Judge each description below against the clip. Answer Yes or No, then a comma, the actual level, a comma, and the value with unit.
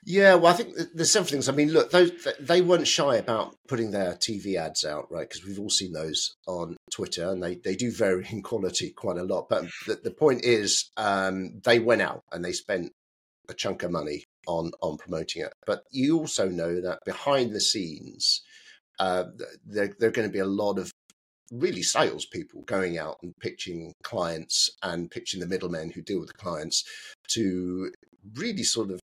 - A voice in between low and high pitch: No, low, 105 Hz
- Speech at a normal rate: Yes, average, 195 wpm